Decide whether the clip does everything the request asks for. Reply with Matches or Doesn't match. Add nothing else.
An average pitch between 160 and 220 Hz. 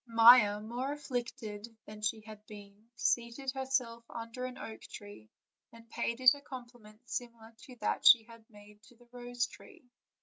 Doesn't match